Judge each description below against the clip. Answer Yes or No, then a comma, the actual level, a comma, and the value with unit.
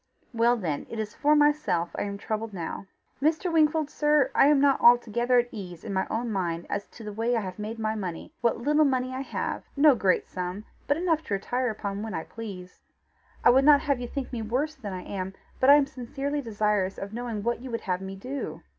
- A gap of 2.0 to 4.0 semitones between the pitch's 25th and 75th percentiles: No, wide, 5.5 semitones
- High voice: Yes, high, 230 Hz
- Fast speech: Yes, fast, 230 wpm